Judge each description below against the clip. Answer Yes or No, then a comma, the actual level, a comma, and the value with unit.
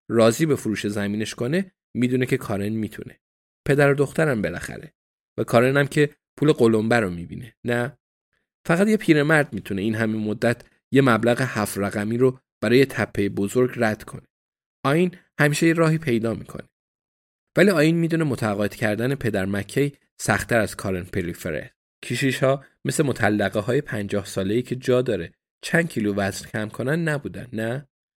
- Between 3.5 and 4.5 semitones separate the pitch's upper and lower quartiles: No, average, 5.2 semitones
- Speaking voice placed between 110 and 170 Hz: Yes, low, 120 Hz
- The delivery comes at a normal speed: No, fast, 160 wpm